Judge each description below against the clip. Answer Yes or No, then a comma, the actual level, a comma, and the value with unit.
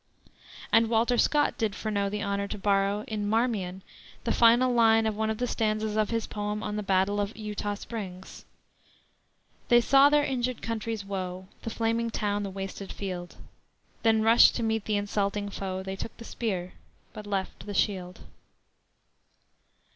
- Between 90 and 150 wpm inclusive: No, average, 165 wpm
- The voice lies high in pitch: Yes, high, 210 Hz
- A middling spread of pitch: No, narrow, 2.3 semitones